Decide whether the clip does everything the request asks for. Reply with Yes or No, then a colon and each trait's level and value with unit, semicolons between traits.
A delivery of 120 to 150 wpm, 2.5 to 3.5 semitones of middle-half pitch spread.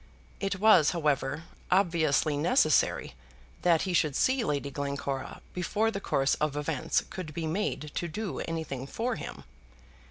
No: average, 145 wpm; average, 5.1 semitones